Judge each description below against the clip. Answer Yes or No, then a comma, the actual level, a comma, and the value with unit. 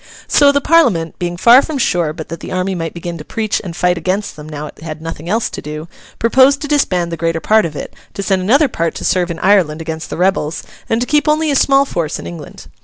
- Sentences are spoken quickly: Yes, fast, 250 wpm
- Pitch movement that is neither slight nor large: No, wide, 6.4 semitones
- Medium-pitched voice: Yes, medium, 180 Hz